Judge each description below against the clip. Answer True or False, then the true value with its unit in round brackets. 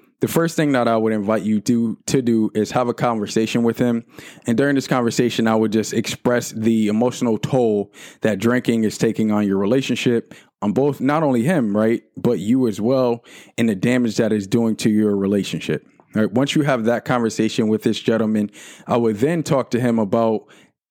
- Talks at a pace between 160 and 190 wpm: False (205 wpm)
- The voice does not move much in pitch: True (2.2 semitones)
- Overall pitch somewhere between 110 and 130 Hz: True (115 Hz)